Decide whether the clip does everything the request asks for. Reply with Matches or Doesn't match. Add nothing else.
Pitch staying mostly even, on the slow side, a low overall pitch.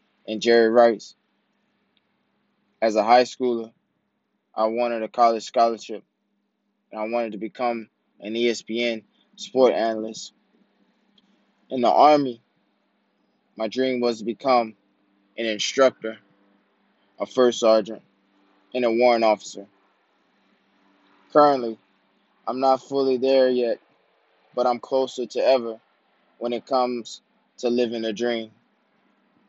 Matches